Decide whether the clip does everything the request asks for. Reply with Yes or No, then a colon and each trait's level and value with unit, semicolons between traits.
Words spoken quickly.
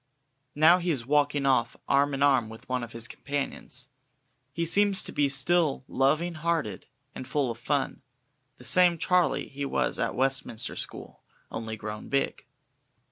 No: average, 160 wpm